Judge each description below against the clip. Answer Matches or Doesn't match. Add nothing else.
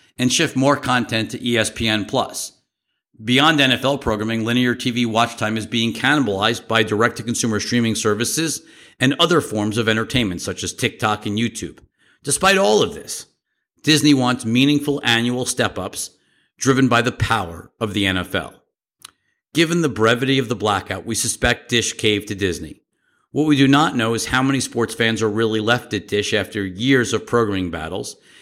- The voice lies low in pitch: Matches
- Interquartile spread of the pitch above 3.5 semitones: Doesn't match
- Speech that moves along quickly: Doesn't match